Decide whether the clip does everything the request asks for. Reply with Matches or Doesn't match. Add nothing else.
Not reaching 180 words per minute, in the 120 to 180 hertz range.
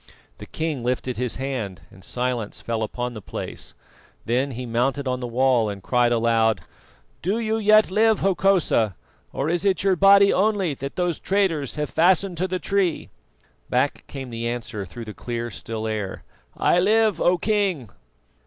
Matches